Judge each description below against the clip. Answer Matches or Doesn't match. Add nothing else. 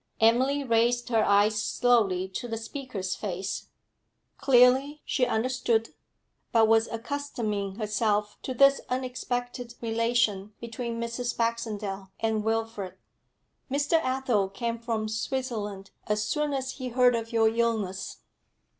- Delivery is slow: Matches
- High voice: Matches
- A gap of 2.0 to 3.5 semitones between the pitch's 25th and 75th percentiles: Matches